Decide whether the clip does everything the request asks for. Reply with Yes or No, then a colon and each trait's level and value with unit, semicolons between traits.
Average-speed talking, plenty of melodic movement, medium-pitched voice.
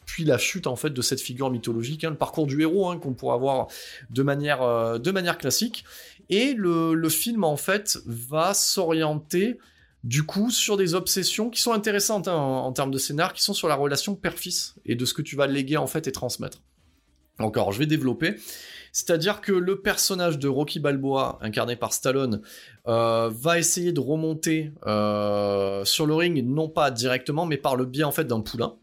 Yes: average, 200 wpm; wide, 6.0 semitones; medium, 150 Hz